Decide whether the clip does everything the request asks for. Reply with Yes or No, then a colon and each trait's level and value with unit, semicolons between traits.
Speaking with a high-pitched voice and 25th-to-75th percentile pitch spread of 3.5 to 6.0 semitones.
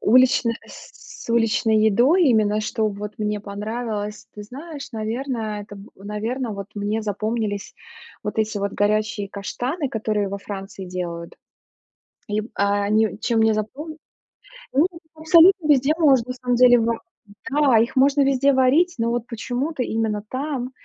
Yes: high, 225 Hz; average, 3.8 semitones